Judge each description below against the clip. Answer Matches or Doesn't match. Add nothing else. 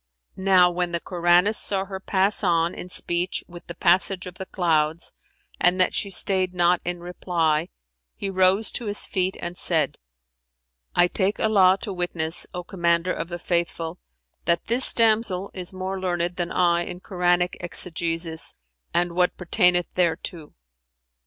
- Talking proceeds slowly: Doesn't match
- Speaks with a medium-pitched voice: Matches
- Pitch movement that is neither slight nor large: Doesn't match